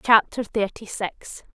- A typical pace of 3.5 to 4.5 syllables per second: Yes, 3.7 syllables/s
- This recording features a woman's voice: Yes, female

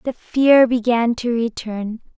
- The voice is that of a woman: Yes, female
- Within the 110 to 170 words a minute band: Yes, slow, 135 wpm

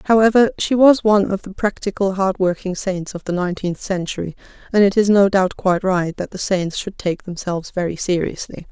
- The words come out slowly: No, average, 195 wpm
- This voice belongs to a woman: Yes, female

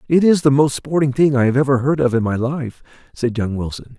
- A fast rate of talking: Yes, fast, 240 wpm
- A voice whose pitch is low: Yes, low, 130 Hz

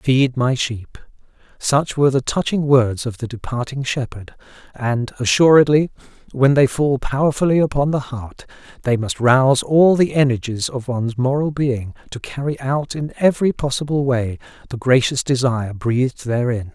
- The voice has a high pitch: No, low, 130 Hz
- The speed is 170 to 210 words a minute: No, average, 155 wpm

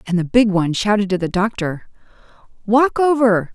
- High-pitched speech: Yes, high, 205 Hz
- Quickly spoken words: No, average, 170 wpm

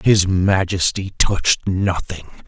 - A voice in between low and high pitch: No, very low, 95 Hz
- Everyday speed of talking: No, slow, 95 wpm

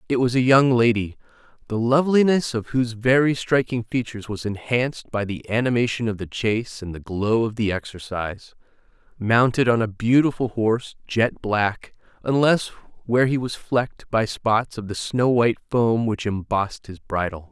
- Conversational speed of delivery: Yes, average, 170 wpm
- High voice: No, low, 115 Hz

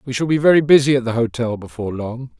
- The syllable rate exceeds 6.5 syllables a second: Yes, 6.7 syllables/s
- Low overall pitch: Yes, low, 125 Hz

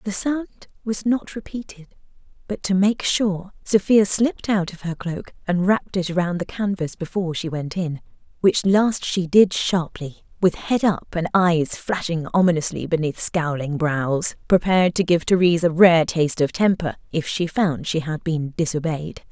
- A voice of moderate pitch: Yes, medium, 180 Hz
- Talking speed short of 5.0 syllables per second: Yes, 4.6 syllables/s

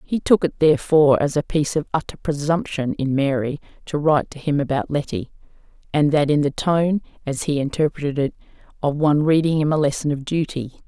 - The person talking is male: No, female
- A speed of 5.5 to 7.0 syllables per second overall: Yes, 6.0 syllables/s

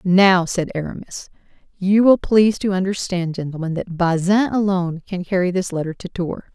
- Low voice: No, medium, 185 Hz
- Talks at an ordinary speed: Yes, average, 165 wpm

